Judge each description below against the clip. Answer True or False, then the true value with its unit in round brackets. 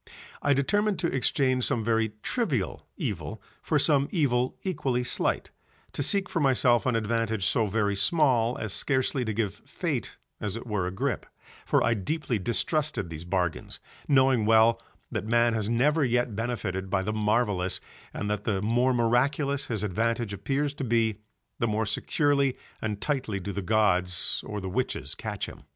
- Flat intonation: False (4.3 semitones)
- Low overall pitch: True (115 Hz)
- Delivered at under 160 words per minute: False (170 wpm)